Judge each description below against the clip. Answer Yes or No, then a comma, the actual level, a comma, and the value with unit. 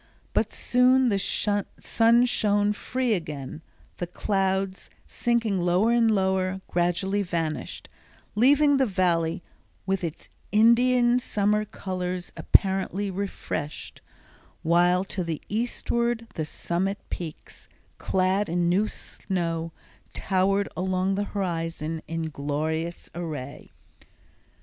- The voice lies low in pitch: No, high, 190 Hz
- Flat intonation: No, average, 3.5 semitones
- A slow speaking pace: Yes, slow, 105 wpm